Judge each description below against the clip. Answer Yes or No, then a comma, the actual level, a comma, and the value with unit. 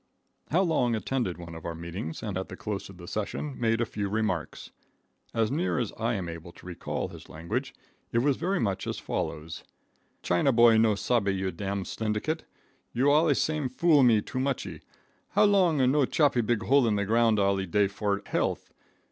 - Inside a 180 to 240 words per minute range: Yes, average, 190 wpm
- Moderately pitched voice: No, low, 110 Hz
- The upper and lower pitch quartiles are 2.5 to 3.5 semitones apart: No, wide, 5.5 semitones